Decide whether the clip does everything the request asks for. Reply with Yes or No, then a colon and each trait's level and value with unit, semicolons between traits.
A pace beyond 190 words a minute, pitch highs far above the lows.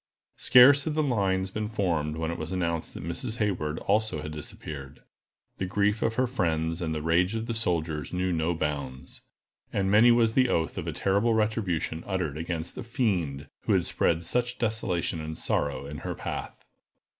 No: average, 185 wpm; wide, 5.7 semitones